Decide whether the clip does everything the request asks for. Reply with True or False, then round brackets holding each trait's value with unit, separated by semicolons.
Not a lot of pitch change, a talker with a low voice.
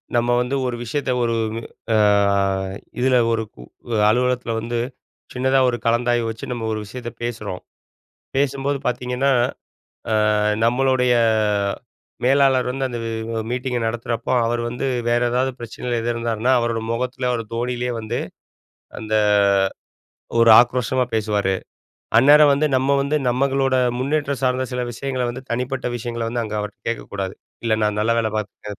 True (2.1 semitones; 120 Hz)